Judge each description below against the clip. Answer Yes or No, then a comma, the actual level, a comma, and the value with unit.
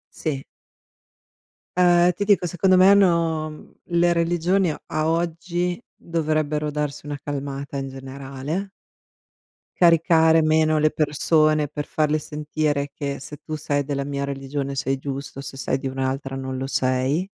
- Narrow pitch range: No, average, 3.2 semitones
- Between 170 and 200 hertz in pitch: No, medium, 150 Hz